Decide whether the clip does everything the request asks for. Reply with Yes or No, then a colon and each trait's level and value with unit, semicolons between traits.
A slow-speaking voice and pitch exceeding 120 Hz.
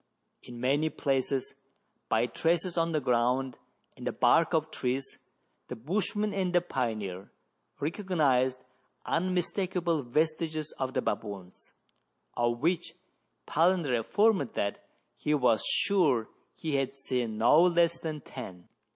Yes: slow, 130 wpm; medium, 140 Hz